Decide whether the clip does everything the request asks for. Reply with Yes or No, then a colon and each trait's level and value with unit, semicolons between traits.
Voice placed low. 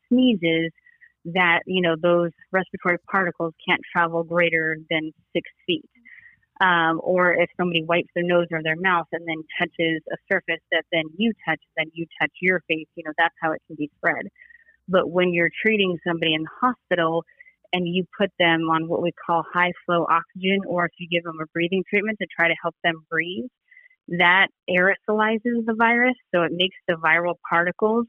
No: medium, 175 Hz